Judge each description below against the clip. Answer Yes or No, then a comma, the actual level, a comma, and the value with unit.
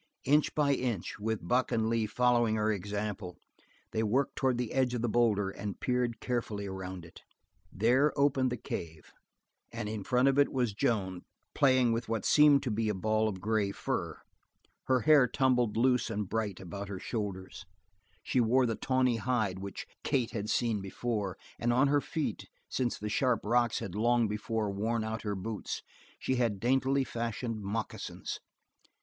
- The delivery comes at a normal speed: Yes, average, 175 wpm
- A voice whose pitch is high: No, low, 115 Hz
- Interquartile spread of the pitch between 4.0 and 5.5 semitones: No, average, 3.3 semitones